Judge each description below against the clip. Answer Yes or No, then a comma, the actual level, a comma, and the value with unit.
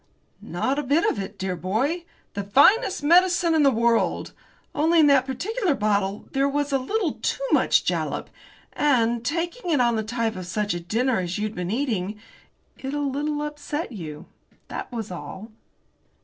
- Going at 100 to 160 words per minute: No, average, 175 wpm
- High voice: Yes, very high, 260 Hz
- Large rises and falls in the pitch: Yes, wide, 6.1 semitones